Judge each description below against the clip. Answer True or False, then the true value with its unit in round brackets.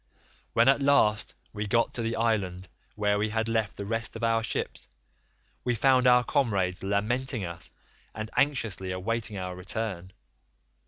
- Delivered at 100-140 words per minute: False (155 wpm)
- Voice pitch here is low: True (110 Hz)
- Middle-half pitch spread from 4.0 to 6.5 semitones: False (3.0 semitones)